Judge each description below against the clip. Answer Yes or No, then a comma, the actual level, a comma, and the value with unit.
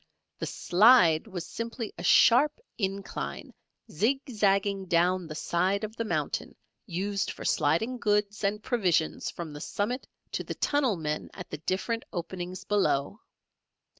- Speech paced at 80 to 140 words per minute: Yes, slow, 135 wpm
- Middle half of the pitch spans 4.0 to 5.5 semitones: Yes, average, 4.4 semitones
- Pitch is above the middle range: Yes, high, 195 Hz